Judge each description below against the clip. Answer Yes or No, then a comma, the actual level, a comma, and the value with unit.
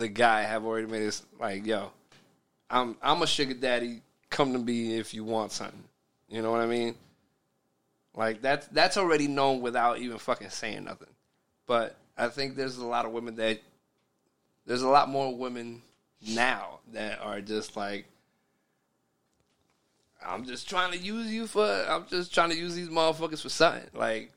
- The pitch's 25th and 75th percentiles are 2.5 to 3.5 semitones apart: No, average, 4.3 semitones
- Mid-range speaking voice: No, low, 120 Hz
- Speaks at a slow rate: No, average, 175 wpm